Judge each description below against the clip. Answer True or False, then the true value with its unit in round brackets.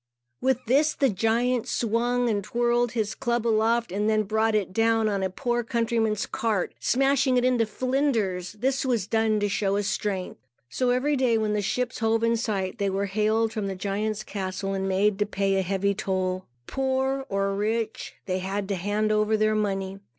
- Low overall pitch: False (215 Hz)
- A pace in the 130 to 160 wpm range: False (185 wpm)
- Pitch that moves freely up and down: False (3.2 semitones)